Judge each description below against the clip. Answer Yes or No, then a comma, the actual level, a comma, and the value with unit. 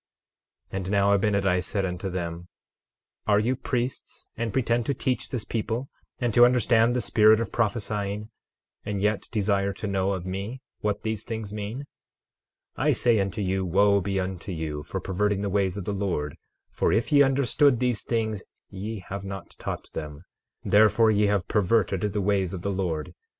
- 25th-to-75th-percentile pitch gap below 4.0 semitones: Yes, average, 2.8 semitones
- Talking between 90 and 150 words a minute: No, average, 180 wpm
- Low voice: Yes, low, 100 Hz